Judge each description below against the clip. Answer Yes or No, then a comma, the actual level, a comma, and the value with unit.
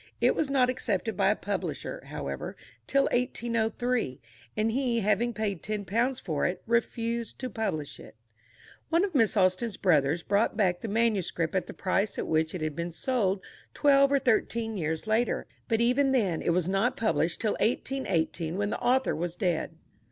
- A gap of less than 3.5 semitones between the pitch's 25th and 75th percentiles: No, average, 5.1 semitones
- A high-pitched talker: Yes, high, 215 Hz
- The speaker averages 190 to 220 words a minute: No, average, 175 wpm